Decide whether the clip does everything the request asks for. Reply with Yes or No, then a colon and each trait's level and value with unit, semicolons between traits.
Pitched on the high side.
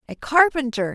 Yes: very high, 275 Hz